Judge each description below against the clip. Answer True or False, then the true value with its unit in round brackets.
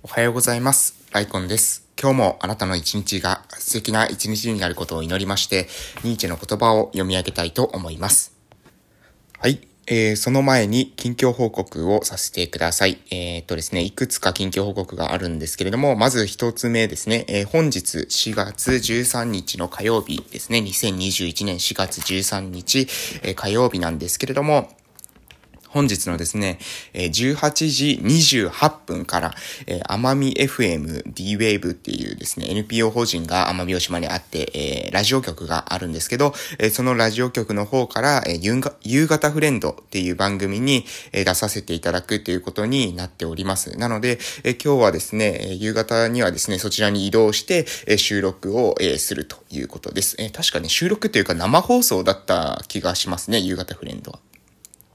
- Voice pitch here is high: False (105 Hz)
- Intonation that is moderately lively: True (5.0 semitones)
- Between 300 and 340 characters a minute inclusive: True (330 characters per minute)